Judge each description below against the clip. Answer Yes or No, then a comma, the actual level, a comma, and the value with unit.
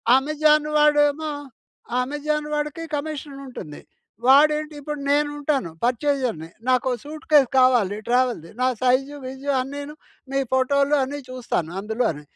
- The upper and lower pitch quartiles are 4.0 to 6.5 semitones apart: No, average, 2.8 semitones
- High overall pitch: Yes, very high, 275 Hz